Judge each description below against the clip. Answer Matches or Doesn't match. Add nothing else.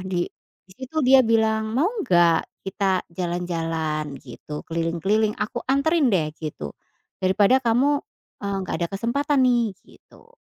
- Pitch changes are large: Matches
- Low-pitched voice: Doesn't match